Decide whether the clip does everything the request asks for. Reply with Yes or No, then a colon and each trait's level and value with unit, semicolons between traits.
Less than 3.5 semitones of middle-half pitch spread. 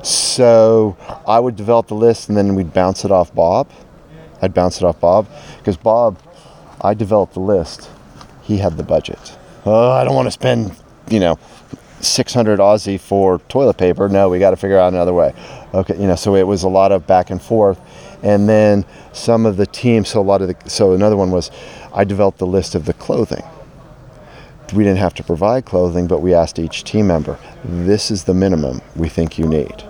Yes: average, 2.8 semitones